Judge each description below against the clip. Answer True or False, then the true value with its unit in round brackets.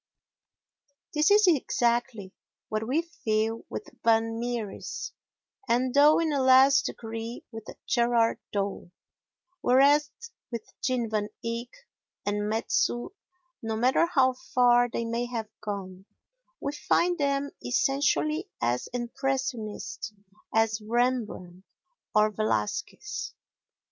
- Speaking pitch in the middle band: False (240 Hz)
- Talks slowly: True (110 wpm)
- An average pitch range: True (3.5 semitones)